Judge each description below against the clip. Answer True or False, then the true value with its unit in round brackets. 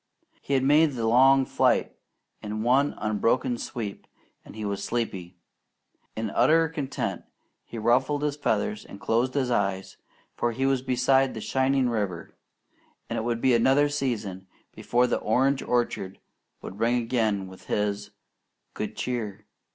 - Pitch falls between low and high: False (120 Hz)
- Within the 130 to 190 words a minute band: True (150 wpm)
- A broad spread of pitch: False (4.0 semitones)